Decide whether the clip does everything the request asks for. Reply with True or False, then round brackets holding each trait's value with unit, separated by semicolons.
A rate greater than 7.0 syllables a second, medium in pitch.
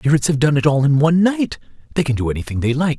True (7.4 syllables/s; 145 Hz)